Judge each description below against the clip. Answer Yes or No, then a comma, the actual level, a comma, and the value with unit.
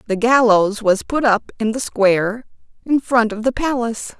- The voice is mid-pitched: No, high, 230 Hz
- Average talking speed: Yes, average, 185 wpm